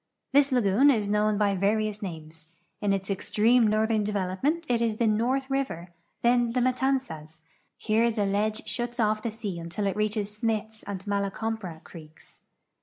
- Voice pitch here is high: Yes, high, 215 Hz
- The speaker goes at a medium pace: Yes, average, 170 wpm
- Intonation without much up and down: No, average, 3.0 semitones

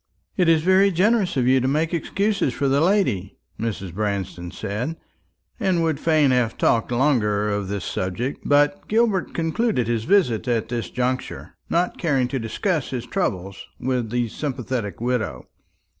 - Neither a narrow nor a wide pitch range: No, wide, 6.9 semitones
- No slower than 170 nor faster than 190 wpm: No, average, 160 wpm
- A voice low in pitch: Yes, low, 130 Hz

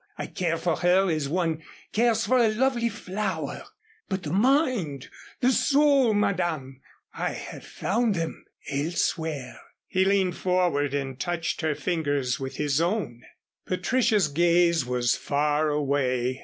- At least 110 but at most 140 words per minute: Yes, slow, 135 wpm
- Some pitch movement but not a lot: No, wide, 5.9 semitones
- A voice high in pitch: No, medium, 170 Hz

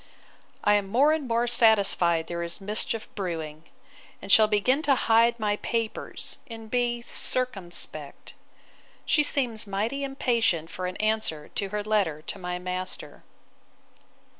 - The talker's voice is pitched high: Yes, high, 215 Hz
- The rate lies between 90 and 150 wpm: Yes, average, 140 wpm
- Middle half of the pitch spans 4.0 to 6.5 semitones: Yes, average, 4.5 semitones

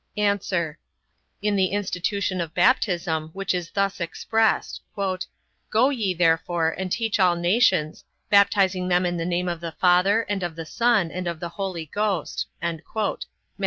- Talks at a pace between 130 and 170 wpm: Yes, average, 155 wpm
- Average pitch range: Yes, average, 3.0 semitones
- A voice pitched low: No, medium, 185 Hz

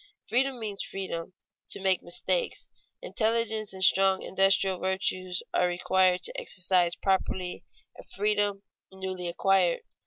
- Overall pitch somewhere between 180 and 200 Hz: Yes, high, 190 Hz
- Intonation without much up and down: Yes, narrow, 1.9 semitones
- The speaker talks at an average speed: No, slow, 120 wpm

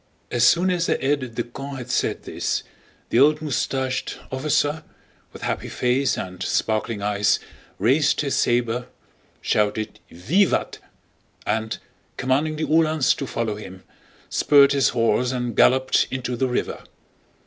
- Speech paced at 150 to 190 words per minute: No, slow, 135 wpm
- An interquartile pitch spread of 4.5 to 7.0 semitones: No, average, 3.8 semitones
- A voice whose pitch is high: No, low, 130 Hz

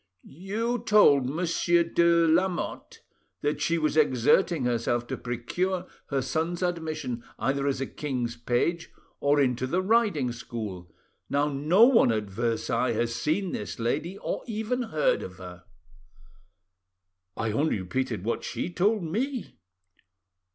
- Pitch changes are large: Yes, wide, 6.7 semitones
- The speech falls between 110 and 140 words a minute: Yes, slow, 135 wpm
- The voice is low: No, medium, 145 Hz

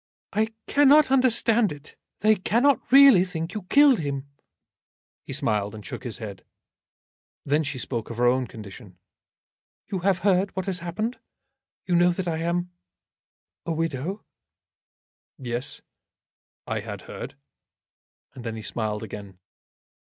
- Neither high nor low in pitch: Yes, medium, 170 Hz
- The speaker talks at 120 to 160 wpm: Yes, slow, 135 wpm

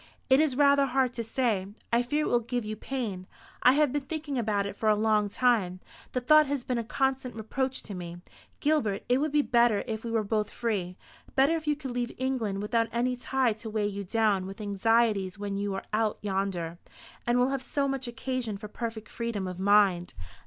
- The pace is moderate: No, fast, 215 wpm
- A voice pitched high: Yes, high, 230 Hz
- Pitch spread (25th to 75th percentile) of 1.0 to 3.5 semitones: No, average, 4.2 semitones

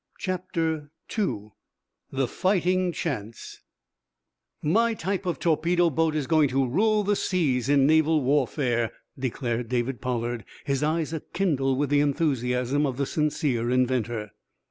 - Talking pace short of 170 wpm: Yes, slow, 135 wpm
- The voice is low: No, medium, 145 Hz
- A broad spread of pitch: No, average, 4.7 semitones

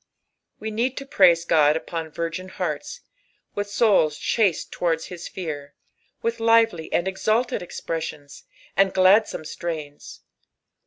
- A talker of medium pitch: Yes, medium, 180 Hz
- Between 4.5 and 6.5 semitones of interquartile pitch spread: Yes, average, 5.1 semitones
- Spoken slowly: Yes, slow, 120 wpm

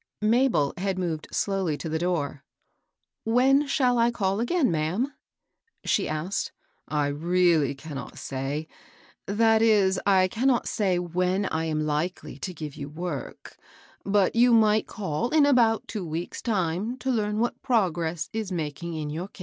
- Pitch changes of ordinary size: No, wide, 6.0 semitones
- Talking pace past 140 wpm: Yes, average, 165 wpm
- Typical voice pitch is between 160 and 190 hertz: Yes, medium, 185 Hz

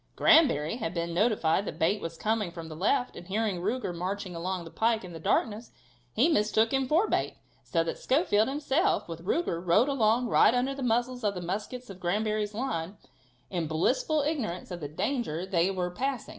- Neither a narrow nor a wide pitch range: No, wide, 6.2 semitones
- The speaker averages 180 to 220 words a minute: Yes, average, 195 wpm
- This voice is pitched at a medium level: No, high, 210 Hz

